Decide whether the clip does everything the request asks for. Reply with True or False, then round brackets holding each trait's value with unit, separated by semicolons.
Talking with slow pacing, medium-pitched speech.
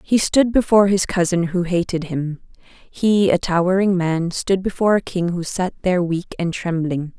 False (185 wpm; 180 Hz)